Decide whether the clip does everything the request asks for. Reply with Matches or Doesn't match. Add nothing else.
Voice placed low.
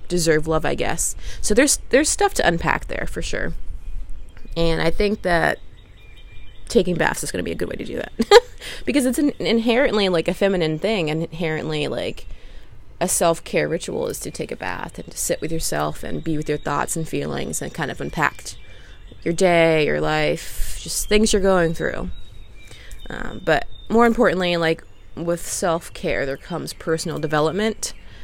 Doesn't match